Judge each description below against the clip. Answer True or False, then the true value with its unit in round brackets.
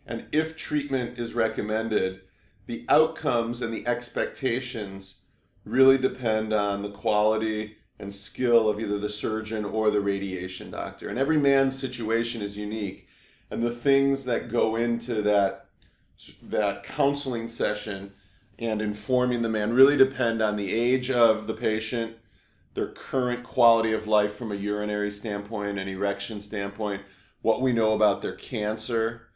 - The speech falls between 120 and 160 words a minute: True (145 wpm)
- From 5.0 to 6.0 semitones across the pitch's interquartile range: False (2.5 semitones)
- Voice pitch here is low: True (110 Hz)